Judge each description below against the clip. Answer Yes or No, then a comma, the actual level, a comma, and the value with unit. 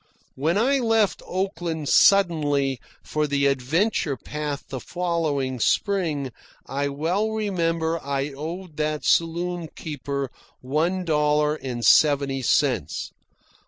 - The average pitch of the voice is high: No, medium, 150 Hz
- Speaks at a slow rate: Yes, slow, 110 wpm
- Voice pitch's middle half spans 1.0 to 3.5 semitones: No, average, 4.0 semitones